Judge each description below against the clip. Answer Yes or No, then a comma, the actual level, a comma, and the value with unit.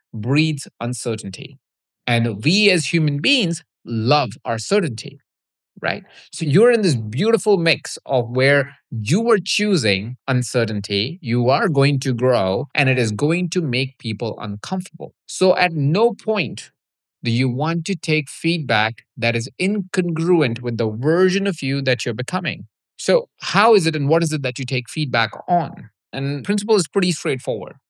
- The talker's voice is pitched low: No, medium, 145 Hz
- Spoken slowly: No, average, 160 wpm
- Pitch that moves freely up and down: Yes, wide, 6.9 semitones